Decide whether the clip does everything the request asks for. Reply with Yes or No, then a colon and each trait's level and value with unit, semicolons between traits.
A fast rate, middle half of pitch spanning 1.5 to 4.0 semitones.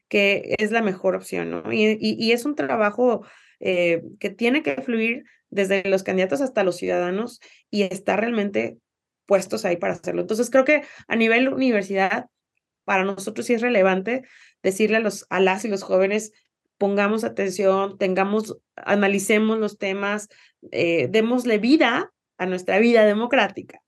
No: average, 155 wpm; average, 3.0 semitones